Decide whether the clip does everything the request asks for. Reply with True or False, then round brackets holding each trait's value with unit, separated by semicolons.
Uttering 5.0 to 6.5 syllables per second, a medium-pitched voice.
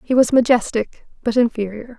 False (5.2 syllables/s; 235 Hz)